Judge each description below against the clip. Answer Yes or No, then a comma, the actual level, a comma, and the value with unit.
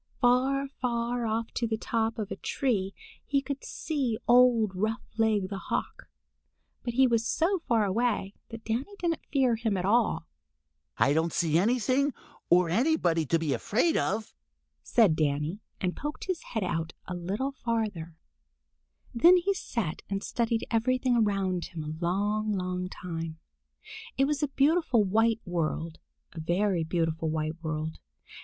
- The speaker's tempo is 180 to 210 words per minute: No, average, 150 wpm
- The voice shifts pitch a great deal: Yes, wide, 5.9 semitones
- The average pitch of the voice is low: No, high, 220 Hz